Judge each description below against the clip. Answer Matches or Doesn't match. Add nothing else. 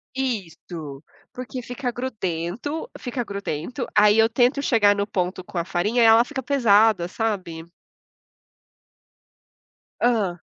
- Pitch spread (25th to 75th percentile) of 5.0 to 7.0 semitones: Matches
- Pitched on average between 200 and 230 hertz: Matches